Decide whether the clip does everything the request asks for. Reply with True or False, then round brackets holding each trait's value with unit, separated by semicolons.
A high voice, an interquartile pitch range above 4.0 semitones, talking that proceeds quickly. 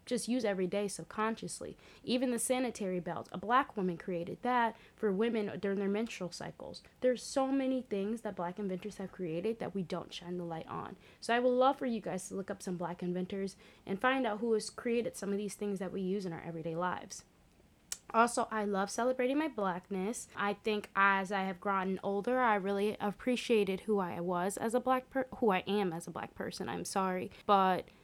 False (200 Hz; 3.7 semitones; 210 wpm)